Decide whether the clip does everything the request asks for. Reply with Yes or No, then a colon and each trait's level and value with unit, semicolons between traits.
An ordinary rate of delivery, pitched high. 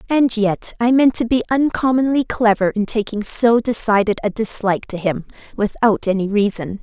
Yes: average, 165 wpm; high, 220 Hz